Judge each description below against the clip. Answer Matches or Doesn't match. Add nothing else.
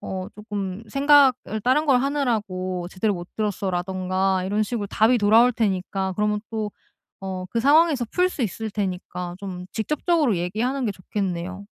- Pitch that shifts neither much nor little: Matches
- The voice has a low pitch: Doesn't match